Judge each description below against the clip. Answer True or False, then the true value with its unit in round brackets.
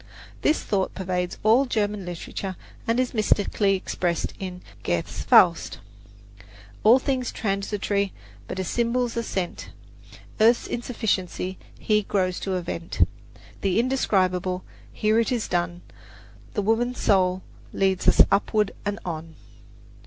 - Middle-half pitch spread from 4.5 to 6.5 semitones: False (3.6 semitones)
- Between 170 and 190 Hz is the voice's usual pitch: False (200 Hz)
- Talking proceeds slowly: True (125 wpm)